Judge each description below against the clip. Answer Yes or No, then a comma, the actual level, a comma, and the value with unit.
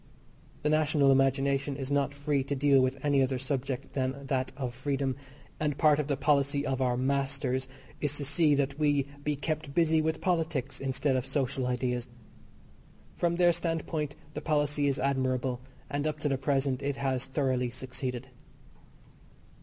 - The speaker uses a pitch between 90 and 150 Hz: Yes, medium, 140 Hz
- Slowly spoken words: No, average, 165 wpm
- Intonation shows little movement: Yes, narrow, 1.9 semitones